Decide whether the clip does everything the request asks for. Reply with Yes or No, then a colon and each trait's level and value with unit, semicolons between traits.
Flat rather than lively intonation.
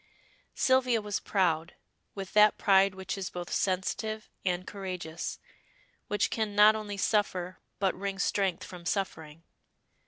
Yes: narrow, 2.3 semitones